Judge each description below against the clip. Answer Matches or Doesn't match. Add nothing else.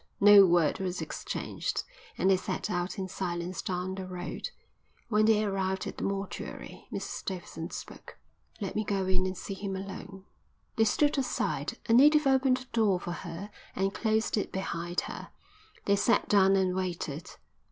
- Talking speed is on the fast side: Doesn't match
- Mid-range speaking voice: Doesn't match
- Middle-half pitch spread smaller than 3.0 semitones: Matches